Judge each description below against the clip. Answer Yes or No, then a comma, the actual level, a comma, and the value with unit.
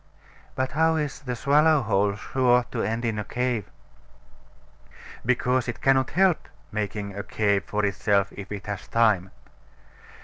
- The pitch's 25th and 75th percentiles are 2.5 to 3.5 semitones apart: No, average, 4.2 semitones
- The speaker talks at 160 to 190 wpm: No, average, 145 wpm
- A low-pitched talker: Yes, low, 115 Hz